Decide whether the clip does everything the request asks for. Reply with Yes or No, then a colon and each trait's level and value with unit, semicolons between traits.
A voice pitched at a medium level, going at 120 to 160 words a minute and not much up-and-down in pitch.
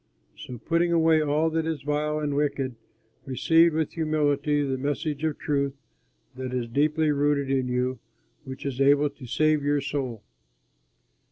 Yes: medium, 145 Hz; average, 155 wpm; narrow, 2.2 semitones